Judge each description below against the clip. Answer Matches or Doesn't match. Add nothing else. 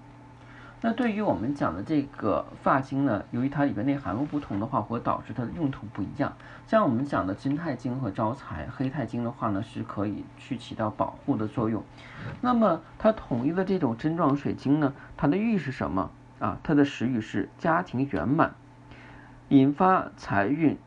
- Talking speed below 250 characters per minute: Doesn't match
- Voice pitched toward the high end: Doesn't match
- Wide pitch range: Doesn't match